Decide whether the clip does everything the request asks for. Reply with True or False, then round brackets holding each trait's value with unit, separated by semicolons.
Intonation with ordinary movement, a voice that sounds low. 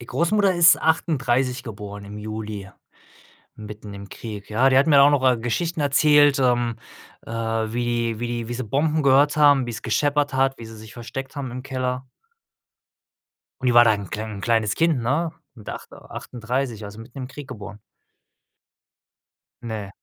True (3.9 semitones; 120 Hz)